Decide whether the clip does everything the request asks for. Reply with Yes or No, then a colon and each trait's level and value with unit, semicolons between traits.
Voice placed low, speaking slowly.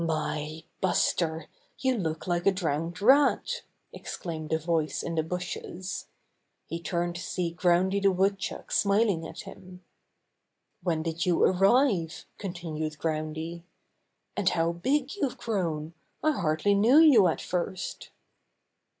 No: medium, 175 Hz; slow, 130 wpm